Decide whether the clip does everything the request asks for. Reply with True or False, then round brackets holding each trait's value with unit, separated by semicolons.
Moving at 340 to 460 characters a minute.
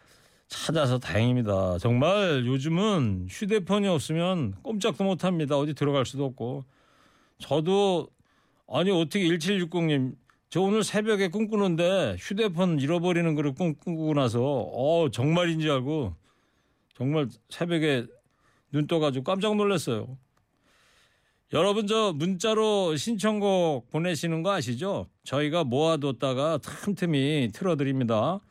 False (265 characters per minute)